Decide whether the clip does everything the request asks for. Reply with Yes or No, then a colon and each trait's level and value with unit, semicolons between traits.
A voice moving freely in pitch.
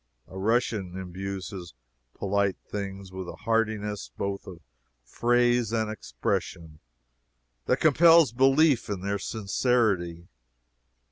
No: average, 4.1 semitones